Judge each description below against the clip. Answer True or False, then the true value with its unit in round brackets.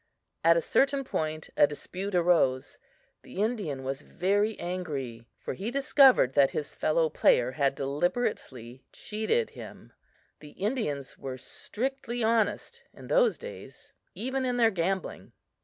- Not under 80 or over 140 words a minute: True (135 wpm)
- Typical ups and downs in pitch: False (8.9 semitones)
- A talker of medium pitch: True (180 Hz)